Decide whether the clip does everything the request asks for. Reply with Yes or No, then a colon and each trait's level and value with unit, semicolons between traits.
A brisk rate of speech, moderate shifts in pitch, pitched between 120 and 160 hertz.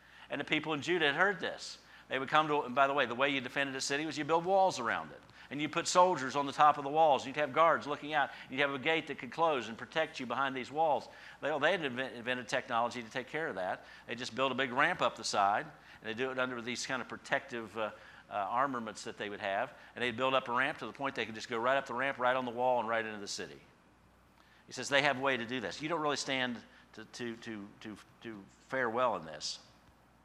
Yes: fast, 280 wpm; average, 3.6 semitones; low, 135 Hz